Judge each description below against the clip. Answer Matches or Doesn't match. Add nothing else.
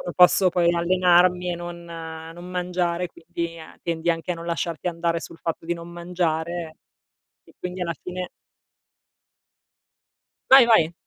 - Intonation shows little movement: Matches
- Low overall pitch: Doesn't match